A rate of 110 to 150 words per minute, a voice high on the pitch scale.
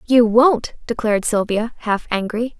Yes: average, 140 wpm; high, 225 Hz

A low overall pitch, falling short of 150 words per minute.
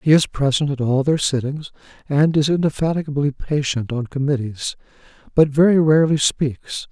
No: medium, 145 Hz; average, 140 wpm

